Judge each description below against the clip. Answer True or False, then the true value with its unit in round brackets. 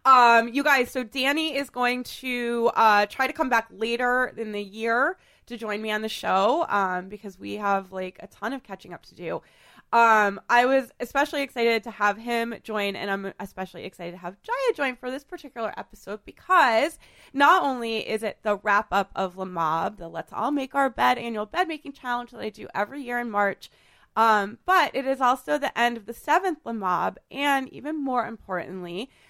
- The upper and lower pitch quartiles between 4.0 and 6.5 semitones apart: True (4.6 semitones)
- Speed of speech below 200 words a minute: False (205 wpm)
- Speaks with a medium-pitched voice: False (230 Hz)